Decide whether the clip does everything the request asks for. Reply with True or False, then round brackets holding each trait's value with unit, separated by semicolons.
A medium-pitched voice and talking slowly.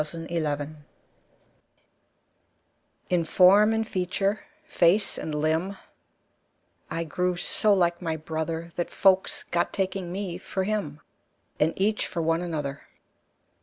True (175 Hz; 130 wpm)